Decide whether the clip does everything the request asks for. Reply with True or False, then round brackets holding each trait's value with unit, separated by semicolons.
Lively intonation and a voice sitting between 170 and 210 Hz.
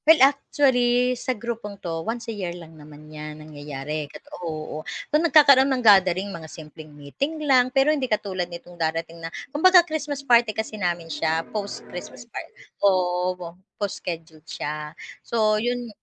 True (7.4 semitones; 190 Hz)